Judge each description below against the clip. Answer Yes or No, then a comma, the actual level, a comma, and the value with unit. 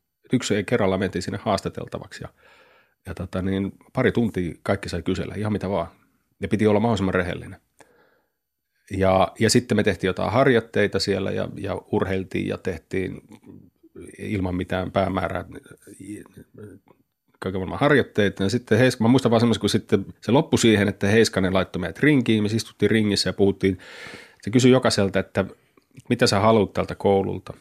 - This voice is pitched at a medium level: No, low, 100 Hz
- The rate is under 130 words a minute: No, average, 150 wpm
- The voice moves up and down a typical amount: Yes, average, 3.1 semitones